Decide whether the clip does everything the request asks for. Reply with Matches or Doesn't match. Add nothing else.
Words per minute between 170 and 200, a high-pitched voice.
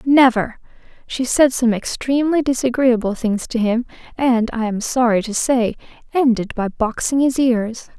Doesn't match